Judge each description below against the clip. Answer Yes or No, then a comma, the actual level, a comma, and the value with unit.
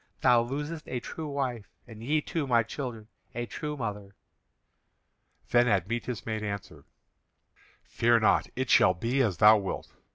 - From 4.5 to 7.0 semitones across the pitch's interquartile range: No, average, 3.7 semitones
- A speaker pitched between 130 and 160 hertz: No, low, 120 Hz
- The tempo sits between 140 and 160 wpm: Yes, average, 150 wpm